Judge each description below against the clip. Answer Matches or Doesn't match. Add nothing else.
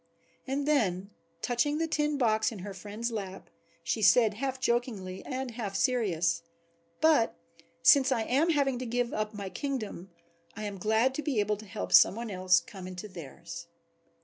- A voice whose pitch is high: Matches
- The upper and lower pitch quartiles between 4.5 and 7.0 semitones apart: Matches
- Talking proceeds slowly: Doesn't match